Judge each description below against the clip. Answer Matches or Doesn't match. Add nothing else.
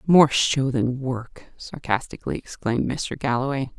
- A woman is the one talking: Matches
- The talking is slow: Matches